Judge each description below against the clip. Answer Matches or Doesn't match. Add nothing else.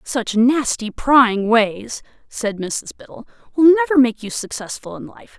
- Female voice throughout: Matches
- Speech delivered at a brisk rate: Doesn't match